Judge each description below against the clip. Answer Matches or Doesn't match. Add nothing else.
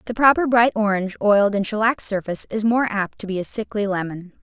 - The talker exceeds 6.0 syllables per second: Matches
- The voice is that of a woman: Matches